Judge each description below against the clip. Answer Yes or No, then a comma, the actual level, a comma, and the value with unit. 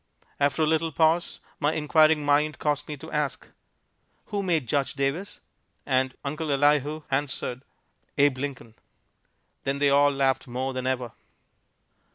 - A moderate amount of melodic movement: No, narrow, 2.3 semitones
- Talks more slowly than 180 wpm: Yes, average, 140 wpm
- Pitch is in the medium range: Yes, medium, 145 Hz